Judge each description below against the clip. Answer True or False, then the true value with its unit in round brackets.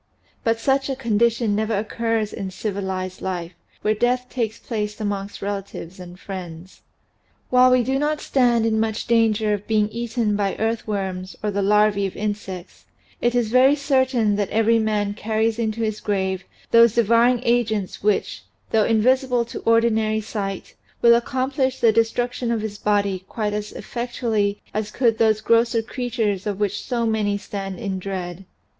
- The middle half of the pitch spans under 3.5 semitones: True (2.5 semitones)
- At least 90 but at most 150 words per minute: False (165 wpm)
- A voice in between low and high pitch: False (220 Hz)